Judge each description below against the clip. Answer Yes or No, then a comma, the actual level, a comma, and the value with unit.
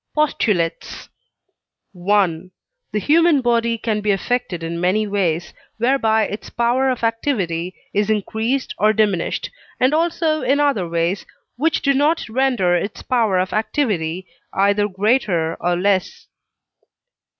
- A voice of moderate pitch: No, high, 215 Hz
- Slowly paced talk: Yes, slow, 130 wpm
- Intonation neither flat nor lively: No, wide, 5.7 semitones